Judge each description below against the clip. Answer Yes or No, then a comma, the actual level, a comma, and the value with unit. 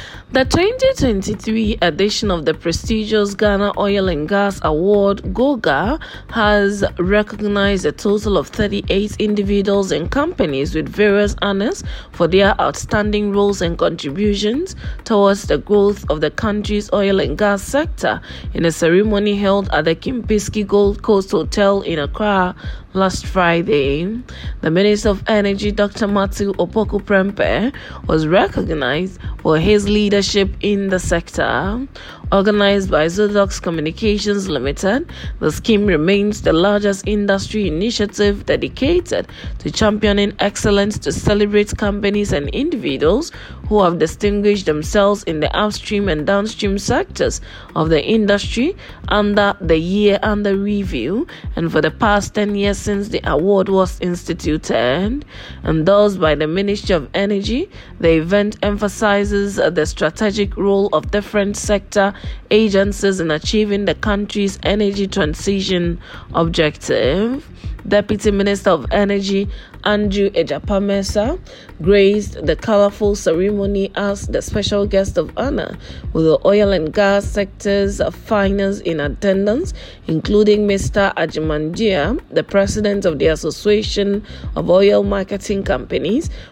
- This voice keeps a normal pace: No, slow, 125 wpm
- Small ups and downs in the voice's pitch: Yes, narrow, 1.4 semitones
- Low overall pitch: No, high, 200 Hz